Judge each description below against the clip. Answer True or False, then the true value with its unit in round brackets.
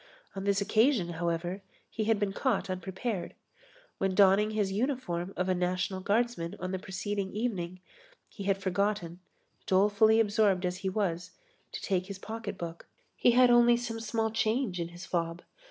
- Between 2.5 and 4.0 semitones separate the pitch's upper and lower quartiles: True (3.3 semitones)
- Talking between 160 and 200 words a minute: True (165 wpm)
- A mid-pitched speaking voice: False (195 Hz)